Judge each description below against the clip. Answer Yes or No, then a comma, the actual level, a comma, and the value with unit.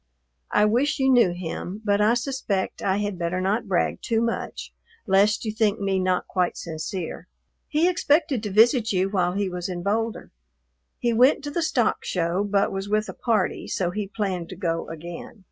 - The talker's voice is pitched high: Yes, high, 205 Hz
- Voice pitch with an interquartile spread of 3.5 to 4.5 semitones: Yes, average, 3.8 semitones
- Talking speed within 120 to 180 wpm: No, average, 190 wpm